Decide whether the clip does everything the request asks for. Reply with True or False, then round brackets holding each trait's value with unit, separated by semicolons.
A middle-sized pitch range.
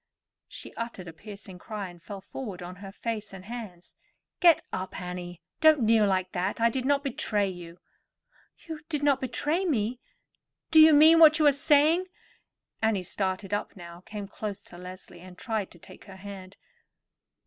False (6.5 semitones)